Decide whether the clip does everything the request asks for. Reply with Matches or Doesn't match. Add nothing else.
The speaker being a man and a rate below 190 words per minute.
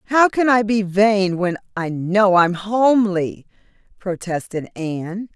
Doesn't match